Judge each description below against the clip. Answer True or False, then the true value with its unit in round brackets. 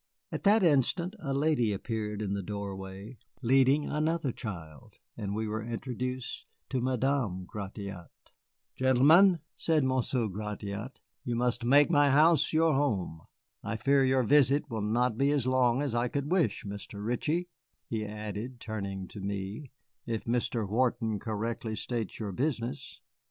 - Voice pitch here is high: False (120 Hz)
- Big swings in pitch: False (4.7 semitones)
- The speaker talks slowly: False (145 wpm)